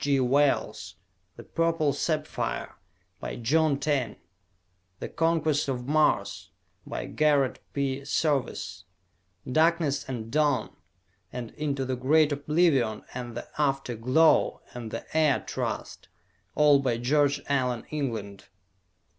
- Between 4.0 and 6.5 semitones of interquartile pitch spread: No, average, 3.4 semitones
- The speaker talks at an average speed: No, slow, 115 wpm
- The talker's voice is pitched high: No, medium, 140 Hz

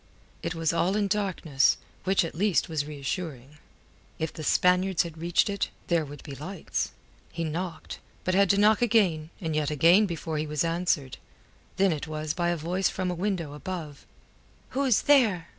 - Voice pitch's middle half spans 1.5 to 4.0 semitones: Yes, average, 3.7 semitones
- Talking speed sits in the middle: Yes, average, 180 wpm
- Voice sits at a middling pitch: Yes, medium, 170 Hz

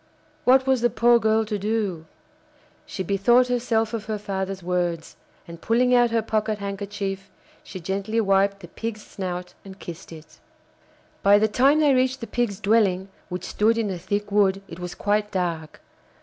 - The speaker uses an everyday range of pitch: Yes, average, 3.1 semitones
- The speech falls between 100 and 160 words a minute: No, average, 175 wpm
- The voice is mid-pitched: No, high, 205 Hz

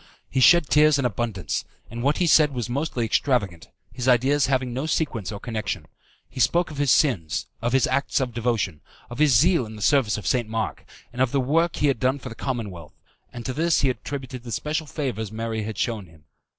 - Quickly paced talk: Yes, fast, 215 wpm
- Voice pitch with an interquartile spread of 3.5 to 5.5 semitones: Yes, average, 4.1 semitones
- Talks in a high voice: No, low, 125 Hz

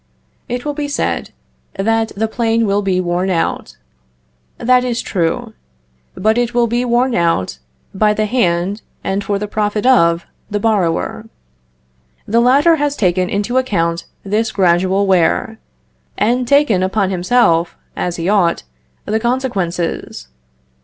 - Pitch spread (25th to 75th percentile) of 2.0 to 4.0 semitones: No, average, 4.8 semitones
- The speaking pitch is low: No, high, 210 Hz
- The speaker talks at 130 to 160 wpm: Yes, average, 140 wpm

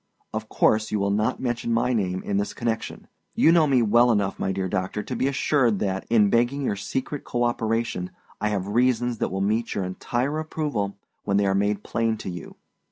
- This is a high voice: No, low, 110 Hz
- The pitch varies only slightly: No, average, 3.5 semitones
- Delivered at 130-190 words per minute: No, fast, 205 wpm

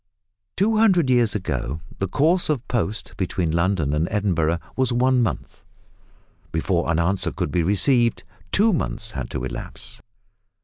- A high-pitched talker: No, low, 100 Hz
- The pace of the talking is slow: No, average, 145 wpm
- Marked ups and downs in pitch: Yes, wide, 7.5 semitones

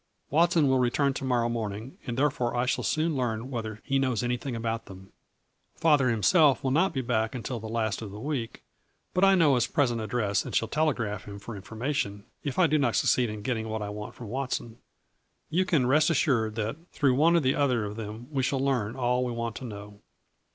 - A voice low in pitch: Yes, low, 125 Hz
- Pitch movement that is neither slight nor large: Yes, average, 3.9 semitones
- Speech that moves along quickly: Yes, fast, 215 wpm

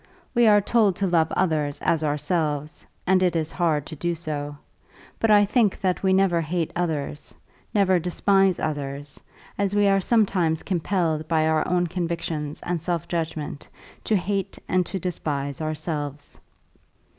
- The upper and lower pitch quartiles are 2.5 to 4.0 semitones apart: Yes, average, 3.6 semitones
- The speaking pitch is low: No, medium, 170 Hz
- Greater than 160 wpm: No, average, 155 wpm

